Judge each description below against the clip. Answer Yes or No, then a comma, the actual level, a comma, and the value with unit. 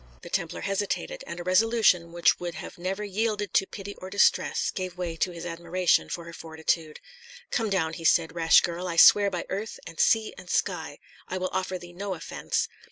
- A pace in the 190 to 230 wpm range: Yes, average, 200 wpm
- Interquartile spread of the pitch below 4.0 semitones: Yes, average, 2.9 semitones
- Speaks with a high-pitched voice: No, medium, 180 Hz